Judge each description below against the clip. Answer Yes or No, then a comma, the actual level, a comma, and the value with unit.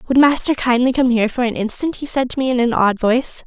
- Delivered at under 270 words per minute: No, fast, 275 wpm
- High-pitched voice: Yes, high, 245 Hz